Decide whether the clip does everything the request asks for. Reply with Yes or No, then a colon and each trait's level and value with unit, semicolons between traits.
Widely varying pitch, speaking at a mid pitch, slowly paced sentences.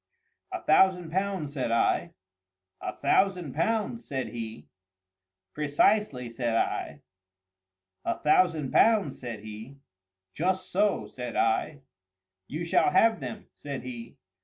Yes: wide, 7.4 semitones; medium, 150 Hz; slow, 115 wpm